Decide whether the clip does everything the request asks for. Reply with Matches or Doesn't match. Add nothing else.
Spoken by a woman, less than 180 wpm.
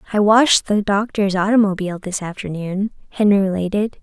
Matches